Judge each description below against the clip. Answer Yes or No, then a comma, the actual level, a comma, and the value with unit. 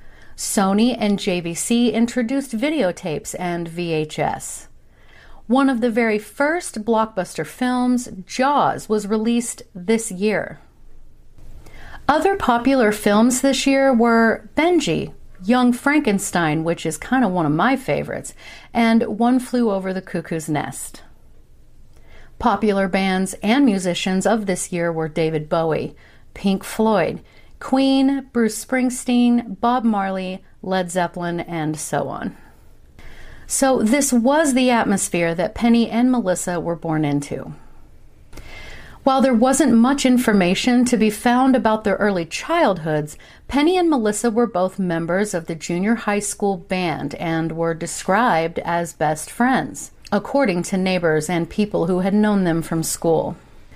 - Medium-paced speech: No, slow, 130 wpm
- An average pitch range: No, wide, 6.1 semitones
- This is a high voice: Yes, high, 210 Hz